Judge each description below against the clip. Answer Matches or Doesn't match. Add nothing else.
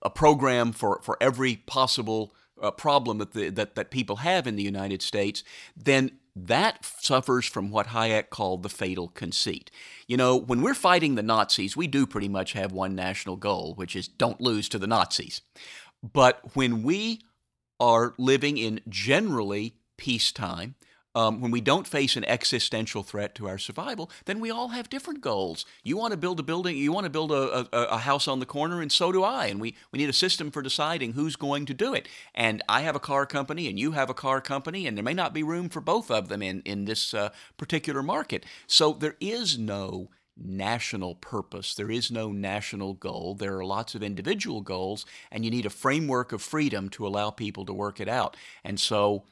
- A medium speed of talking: Doesn't match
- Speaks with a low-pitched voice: Matches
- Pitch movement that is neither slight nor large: Doesn't match